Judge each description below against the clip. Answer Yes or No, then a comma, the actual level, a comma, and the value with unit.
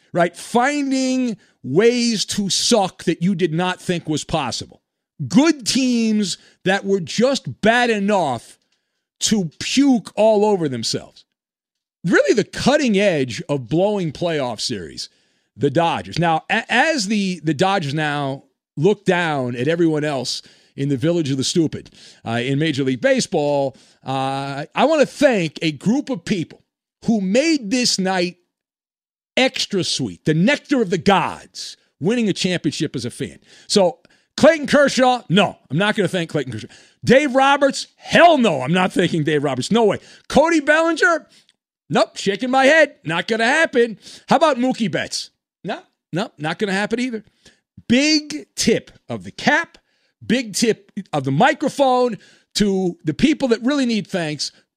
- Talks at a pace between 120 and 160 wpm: Yes, average, 155 wpm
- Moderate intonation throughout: No, wide, 7.7 semitones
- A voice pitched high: Yes, high, 200 Hz